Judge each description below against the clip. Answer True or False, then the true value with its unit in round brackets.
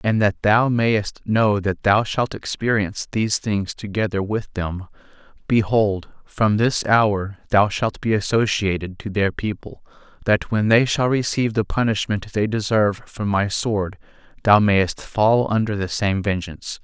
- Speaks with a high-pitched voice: False (105 Hz)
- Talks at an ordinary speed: True (155 wpm)